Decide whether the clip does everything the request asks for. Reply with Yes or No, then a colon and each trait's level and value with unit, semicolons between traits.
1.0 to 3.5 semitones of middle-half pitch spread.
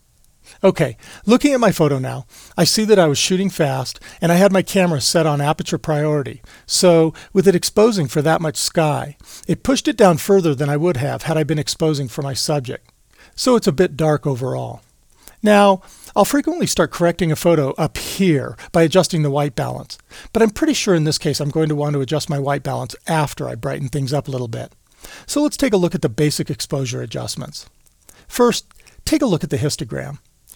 No: average, 4.5 semitones